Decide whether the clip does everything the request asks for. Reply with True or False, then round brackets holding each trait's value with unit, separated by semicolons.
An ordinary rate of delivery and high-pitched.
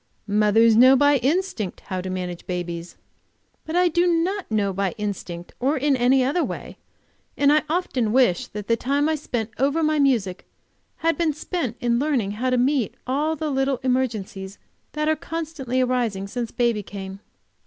True (170 wpm; 255 Hz)